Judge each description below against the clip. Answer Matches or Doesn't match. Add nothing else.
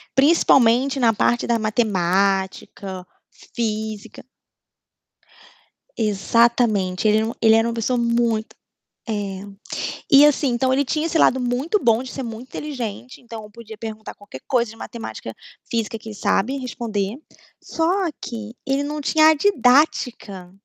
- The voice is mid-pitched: Doesn't match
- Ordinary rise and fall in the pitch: Matches